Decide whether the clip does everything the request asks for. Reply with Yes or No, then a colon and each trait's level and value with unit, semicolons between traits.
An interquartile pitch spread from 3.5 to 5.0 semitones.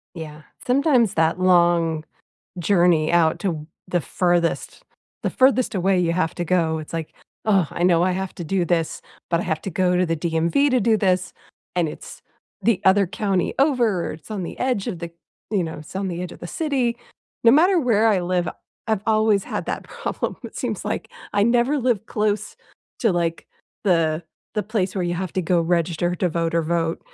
Yes: average, 4.1 semitones